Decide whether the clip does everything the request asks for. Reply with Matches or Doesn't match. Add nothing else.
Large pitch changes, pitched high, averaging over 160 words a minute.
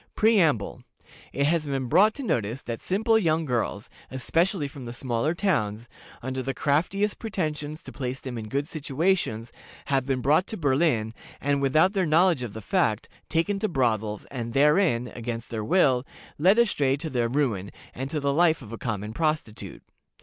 Doesn't match